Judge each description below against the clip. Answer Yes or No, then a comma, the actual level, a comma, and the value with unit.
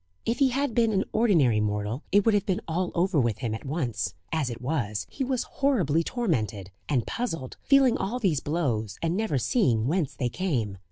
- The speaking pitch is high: No, medium, 160 Hz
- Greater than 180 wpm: Yes, average, 200 wpm